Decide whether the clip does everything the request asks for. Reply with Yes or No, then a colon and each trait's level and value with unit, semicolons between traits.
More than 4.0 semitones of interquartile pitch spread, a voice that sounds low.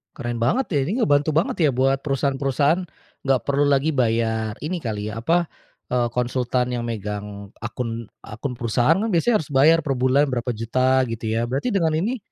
Yes: average, 4.5 semitones; low, 130 Hz